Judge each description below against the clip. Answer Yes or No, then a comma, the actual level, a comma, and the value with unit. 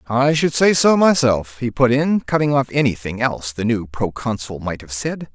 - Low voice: Yes, low, 125 Hz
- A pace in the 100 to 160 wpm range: No, average, 200 wpm